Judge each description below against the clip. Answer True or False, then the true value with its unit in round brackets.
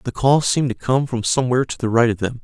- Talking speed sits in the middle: False (295 wpm)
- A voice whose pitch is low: True (125 Hz)